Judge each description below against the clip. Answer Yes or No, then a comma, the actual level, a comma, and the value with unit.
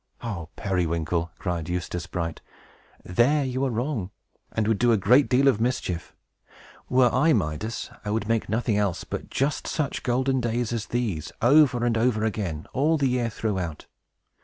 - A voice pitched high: No, low, 115 Hz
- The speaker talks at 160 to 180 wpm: Yes, average, 165 wpm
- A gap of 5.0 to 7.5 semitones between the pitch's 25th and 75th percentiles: Yes, wide, 5.6 semitones